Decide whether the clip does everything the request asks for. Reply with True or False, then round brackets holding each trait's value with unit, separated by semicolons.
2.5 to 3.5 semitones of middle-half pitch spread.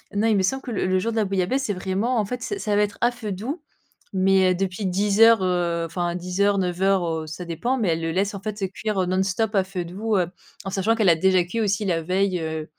True (2.9 semitones)